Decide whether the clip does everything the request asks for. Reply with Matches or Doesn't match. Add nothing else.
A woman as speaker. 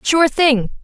Matches